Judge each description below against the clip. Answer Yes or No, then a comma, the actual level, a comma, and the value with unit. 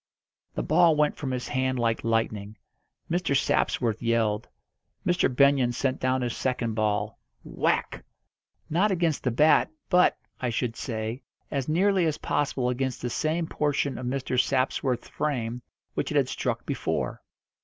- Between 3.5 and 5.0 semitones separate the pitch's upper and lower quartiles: Yes, average, 4.3 semitones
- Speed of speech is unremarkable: Yes, average, 150 wpm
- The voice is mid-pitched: No, low, 130 Hz